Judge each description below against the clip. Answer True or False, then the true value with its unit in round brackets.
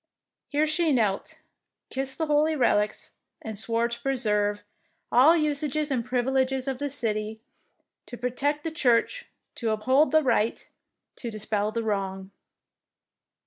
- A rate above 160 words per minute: False (135 wpm)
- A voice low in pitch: False (250 Hz)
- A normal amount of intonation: True (5.0 semitones)